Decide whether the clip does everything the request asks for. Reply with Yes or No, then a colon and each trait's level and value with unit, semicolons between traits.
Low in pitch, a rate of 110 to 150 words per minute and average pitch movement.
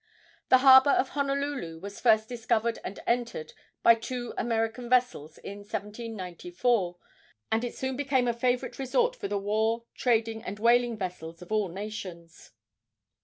No: high, 225 Hz; average, 145 wpm; average, 3.5 semitones